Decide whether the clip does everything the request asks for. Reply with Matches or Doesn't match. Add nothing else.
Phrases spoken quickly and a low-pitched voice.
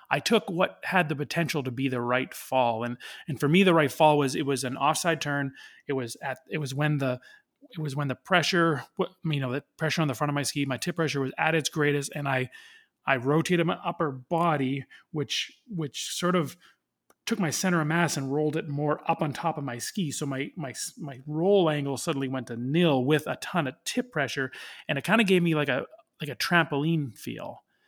Doesn't match